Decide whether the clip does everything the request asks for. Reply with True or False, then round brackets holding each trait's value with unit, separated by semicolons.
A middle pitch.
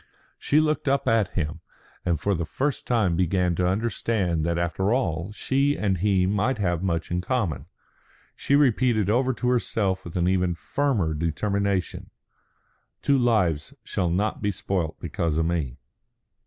False (95 Hz)